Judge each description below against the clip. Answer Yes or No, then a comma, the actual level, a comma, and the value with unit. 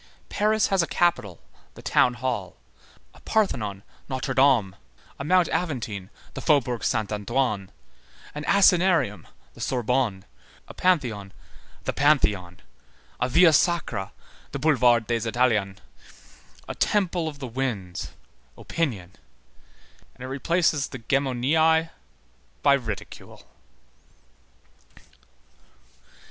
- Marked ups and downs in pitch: Yes, wide, 6.9 semitones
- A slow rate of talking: Yes, slow, 105 wpm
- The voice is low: Yes, low, 130 Hz